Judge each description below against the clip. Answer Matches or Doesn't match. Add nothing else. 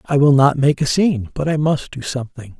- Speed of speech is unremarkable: Doesn't match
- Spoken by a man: Matches